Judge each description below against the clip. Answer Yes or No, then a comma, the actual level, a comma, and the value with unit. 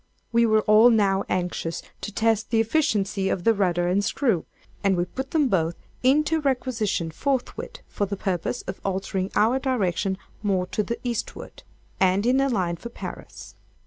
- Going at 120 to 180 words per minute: Yes, average, 170 wpm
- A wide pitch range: No, average, 4.5 semitones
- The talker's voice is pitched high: Yes, high, 210 Hz